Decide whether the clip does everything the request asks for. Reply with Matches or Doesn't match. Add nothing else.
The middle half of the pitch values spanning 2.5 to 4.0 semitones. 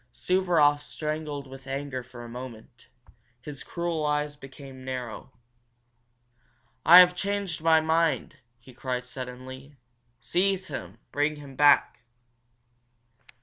Matches